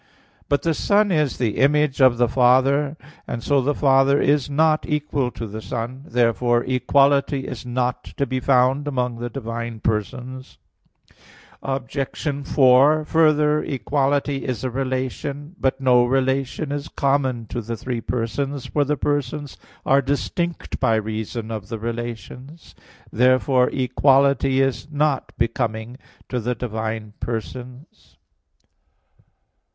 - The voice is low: Yes, low, 130 Hz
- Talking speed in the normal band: No, slow, 130 wpm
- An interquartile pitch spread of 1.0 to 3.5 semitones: Yes, average, 2.8 semitones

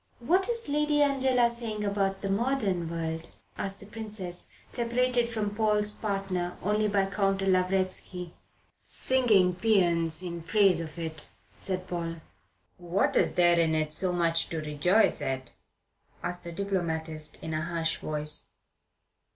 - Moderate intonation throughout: Yes, average, 4.1 semitones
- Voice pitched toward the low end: No, medium, 185 Hz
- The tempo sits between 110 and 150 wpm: Yes, average, 140 wpm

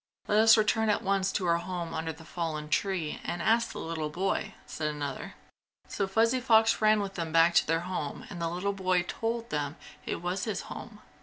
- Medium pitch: Yes, medium, 180 Hz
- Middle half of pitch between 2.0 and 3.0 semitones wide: No, average, 4.4 semitones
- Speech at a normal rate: No, fast, 210 wpm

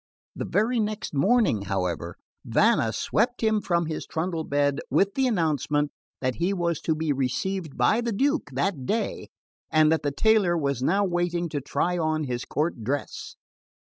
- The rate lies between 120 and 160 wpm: No, average, 170 wpm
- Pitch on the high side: No, medium, 165 Hz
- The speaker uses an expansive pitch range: Yes, wide, 5.8 semitones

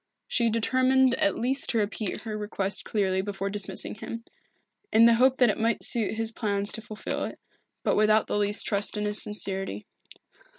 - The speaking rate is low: No, average, 180 wpm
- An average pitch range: No, narrow, 2.2 semitones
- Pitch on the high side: Yes, high, 215 Hz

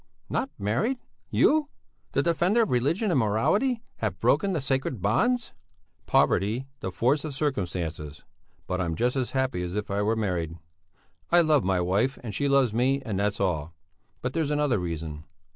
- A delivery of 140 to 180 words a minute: Yes, average, 170 wpm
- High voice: No, low, 120 Hz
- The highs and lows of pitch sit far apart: Yes, wide, 7.9 semitones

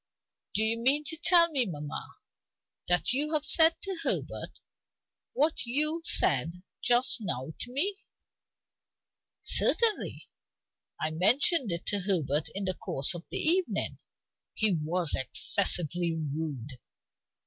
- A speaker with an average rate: No, slow, 125 wpm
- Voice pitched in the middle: No, high, 205 Hz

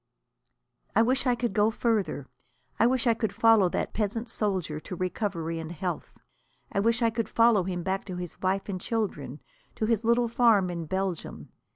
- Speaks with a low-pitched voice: No, high, 205 Hz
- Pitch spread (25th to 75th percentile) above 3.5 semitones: Yes, average, 4.2 semitones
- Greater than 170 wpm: Yes, average, 185 wpm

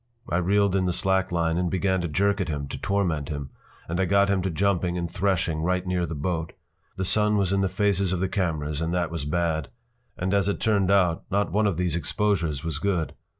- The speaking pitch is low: Yes, very low, 90 Hz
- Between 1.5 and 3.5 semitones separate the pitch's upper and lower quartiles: Yes, average, 3.0 semitones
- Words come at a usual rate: No, fast, 235 wpm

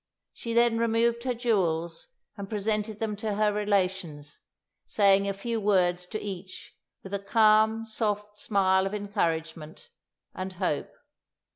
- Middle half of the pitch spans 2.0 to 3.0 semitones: Yes, average, 2.7 semitones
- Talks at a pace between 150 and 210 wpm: No, slow, 135 wpm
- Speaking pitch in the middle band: No, high, 205 Hz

